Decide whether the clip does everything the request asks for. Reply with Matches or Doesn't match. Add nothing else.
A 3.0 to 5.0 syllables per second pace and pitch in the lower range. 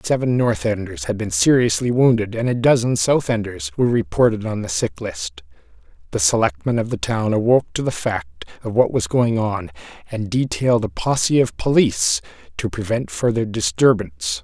Doesn't match